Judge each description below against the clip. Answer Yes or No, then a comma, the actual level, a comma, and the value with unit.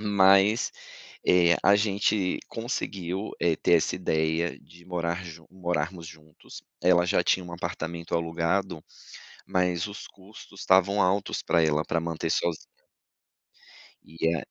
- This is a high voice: No, very low, 90 Hz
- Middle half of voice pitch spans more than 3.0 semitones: No, average, 2.7 semitones